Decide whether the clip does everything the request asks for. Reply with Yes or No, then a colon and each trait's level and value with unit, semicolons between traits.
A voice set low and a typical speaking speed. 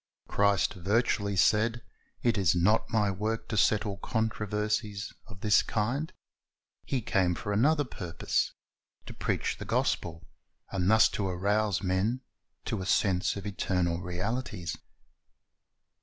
No: low, 100 Hz; slow, 125 wpm